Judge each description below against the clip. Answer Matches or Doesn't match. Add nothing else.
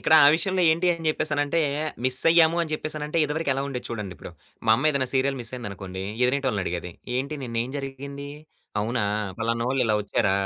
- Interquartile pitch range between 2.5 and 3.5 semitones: Doesn't match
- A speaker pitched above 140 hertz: Doesn't match